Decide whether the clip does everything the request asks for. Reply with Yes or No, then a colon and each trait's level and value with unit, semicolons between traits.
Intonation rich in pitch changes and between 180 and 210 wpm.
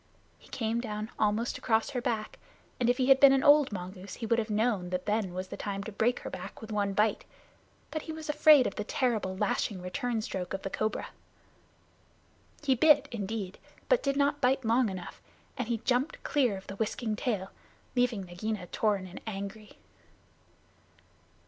No: average, 4.1 semitones; average, 185 wpm